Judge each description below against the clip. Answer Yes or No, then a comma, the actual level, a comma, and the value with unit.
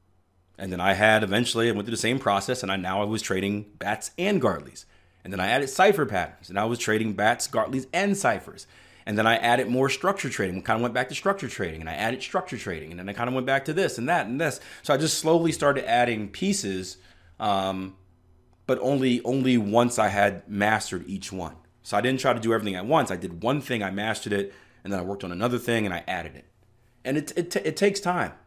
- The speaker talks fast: Yes, fast, 250 wpm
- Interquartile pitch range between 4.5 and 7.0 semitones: Yes, average, 5.0 semitones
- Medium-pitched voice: No, low, 110 Hz